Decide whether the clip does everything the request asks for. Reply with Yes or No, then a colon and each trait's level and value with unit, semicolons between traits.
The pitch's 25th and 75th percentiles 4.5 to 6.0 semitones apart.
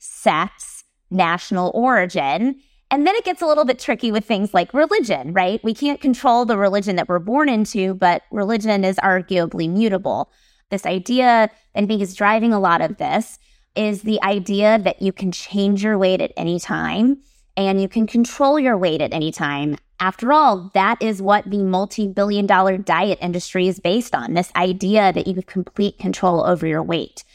No: average, 3.7 semitones